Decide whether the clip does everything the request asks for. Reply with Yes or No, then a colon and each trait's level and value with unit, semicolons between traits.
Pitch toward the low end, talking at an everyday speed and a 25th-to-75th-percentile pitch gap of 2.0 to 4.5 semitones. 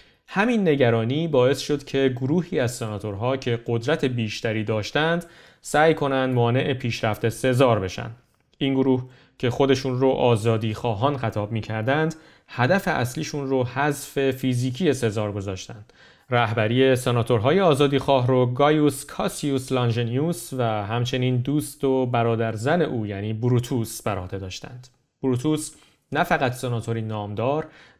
Yes: low, 130 Hz; average, 125 wpm; average, 3.7 semitones